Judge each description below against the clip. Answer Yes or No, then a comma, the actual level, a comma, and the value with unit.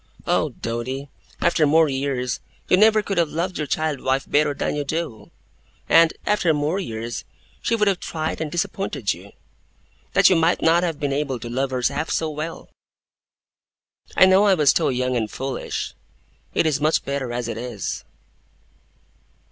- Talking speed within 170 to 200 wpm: Yes, average, 175 wpm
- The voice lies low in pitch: No, medium, 150 Hz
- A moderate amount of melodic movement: Yes, average, 4.1 semitones